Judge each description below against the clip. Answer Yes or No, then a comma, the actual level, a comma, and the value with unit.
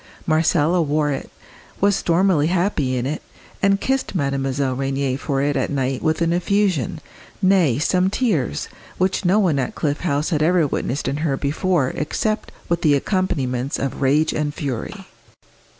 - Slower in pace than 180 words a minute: Yes, average, 160 wpm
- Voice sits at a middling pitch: Yes, medium, 150 Hz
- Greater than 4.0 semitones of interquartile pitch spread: Yes, average, 4.8 semitones